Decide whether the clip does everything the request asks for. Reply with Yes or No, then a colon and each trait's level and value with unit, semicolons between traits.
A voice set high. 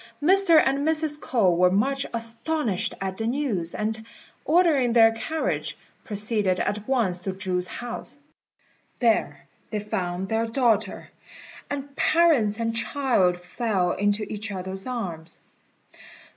Yes: high, 225 Hz